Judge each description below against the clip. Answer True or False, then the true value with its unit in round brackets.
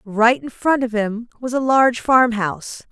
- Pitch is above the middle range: True (235 Hz)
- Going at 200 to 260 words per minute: True (205 wpm)